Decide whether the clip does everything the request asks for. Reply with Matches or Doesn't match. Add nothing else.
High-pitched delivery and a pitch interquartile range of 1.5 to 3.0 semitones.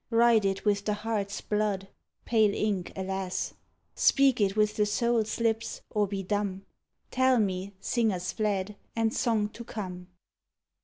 Matches